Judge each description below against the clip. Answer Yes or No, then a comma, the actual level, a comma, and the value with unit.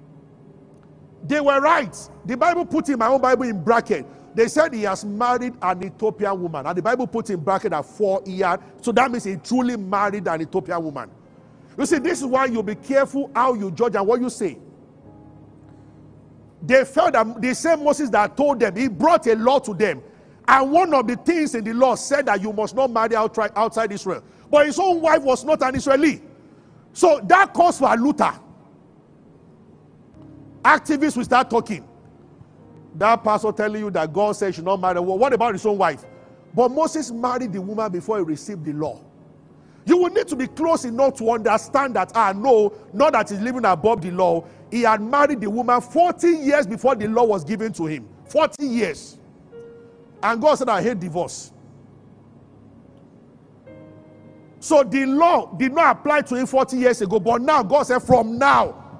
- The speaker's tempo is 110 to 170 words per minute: No, average, 190 wpm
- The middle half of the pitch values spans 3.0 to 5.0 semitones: No, wide, 5.4 semitones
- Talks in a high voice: Yes, high, 235 Hz